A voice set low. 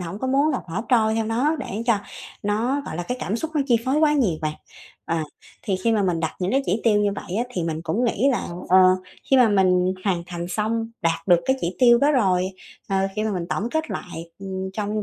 No: high, 210 Hz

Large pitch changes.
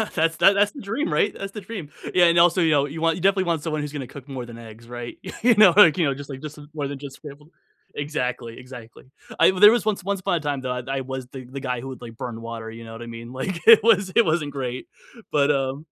Yes: wide, 5.8 semitones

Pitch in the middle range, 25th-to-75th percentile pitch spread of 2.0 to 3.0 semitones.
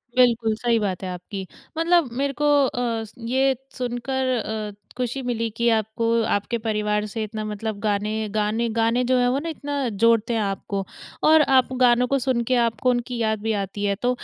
No: high, 230 Hz; average, 2.7 semitones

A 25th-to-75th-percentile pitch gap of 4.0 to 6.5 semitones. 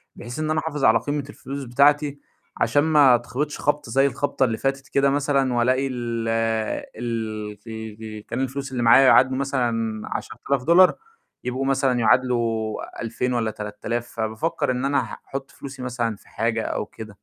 No: average, 3.2 semitones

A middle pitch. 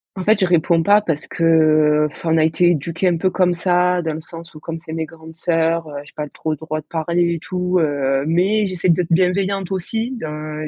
Yes: medium, 165 Hz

